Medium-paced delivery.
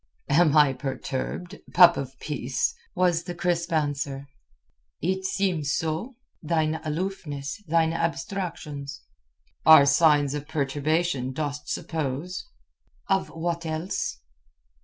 No: slow, 105 wpm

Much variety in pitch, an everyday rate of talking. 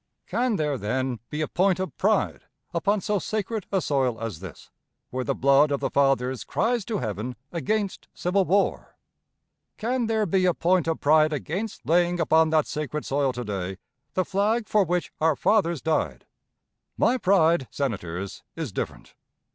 Yes: wide, 6.7 semitones; average, 165 wpm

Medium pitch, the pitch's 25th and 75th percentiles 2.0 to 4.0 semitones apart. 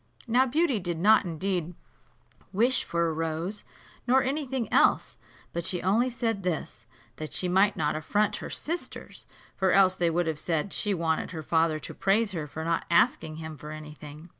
No: medium, 175 Hz; average, 4.8 semitones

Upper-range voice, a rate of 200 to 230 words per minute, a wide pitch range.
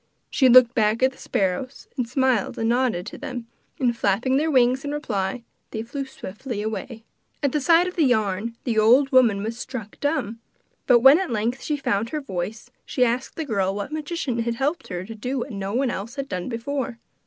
No: high, 240 Hz; fast, 205 wpm; average, 3.9 semitones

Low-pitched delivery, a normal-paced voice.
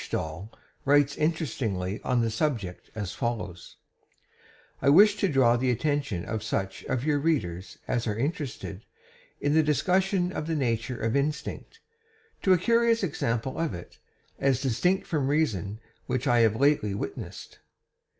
Yes: low, 130 Hz; average, 150 wpm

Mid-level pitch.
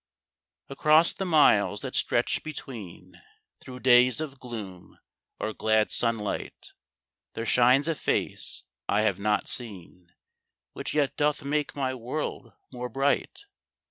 No: low, 125 Hz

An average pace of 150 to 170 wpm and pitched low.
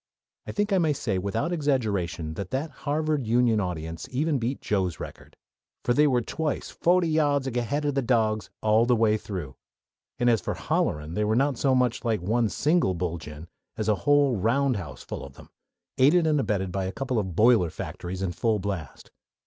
No: average, 195 wpm; low, 115 Hz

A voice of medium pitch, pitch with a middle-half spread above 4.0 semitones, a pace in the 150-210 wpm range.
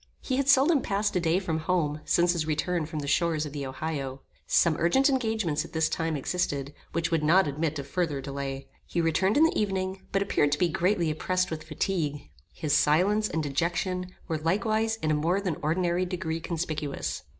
No: medium, 165 Hz; average, 3.7 semitones; average, 195 wpm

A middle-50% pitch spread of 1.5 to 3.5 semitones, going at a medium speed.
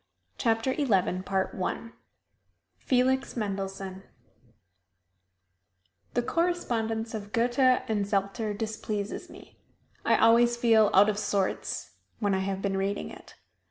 No: average, 3.2 semitones; slow, 110 wpm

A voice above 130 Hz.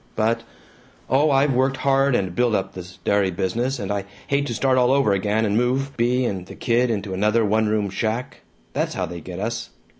No: low, 115 Hz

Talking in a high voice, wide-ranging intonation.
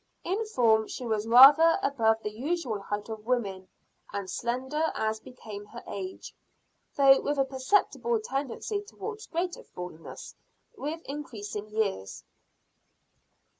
Yes: high, 245 Hz; wide, 5.9 semitones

